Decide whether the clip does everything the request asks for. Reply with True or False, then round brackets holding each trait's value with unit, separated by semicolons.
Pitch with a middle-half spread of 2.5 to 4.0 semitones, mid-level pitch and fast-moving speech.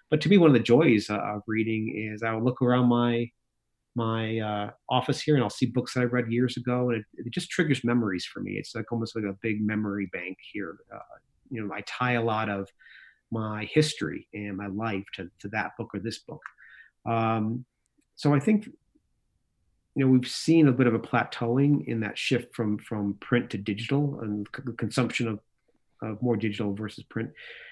False (2.9 semitones; 115 Hz; 210 wpm)